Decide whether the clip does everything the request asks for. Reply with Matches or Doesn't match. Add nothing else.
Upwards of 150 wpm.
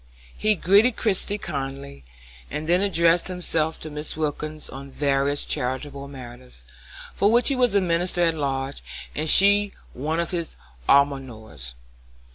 Doesn't match